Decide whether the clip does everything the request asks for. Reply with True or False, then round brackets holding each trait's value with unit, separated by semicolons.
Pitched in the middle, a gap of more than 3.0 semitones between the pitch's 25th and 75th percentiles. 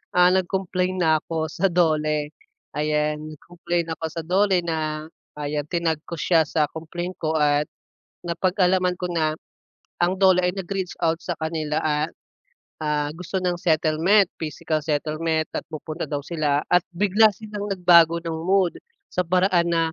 False (165 Hz; 2.7 semitones)